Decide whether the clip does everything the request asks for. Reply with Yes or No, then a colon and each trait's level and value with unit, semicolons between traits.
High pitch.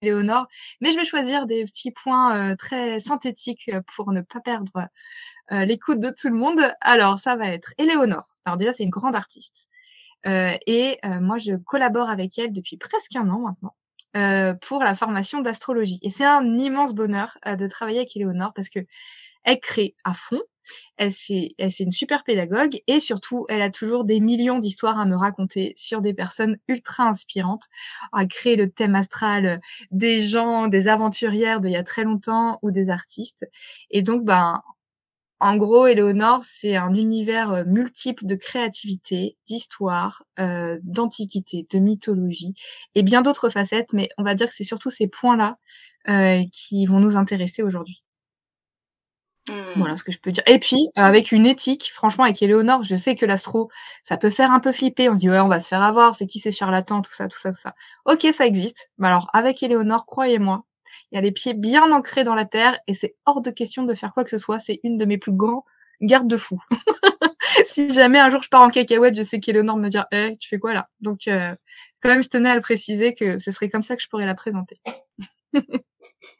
Yes: high, 220 Hz